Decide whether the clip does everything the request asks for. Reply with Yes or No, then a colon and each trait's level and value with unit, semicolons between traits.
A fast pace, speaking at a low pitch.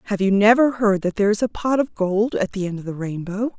No: fast, 285 wpm; high, 205 Hz